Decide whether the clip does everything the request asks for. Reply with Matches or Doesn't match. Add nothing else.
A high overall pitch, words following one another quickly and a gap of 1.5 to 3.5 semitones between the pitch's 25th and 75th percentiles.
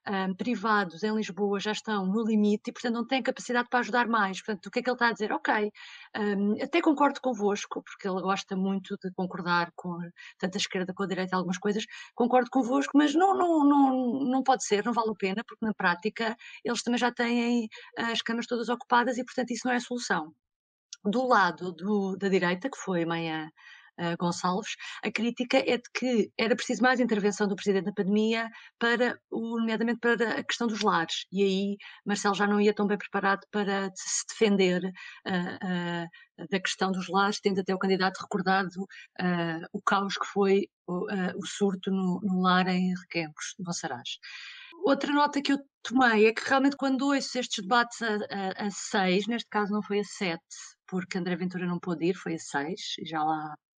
Doesn't match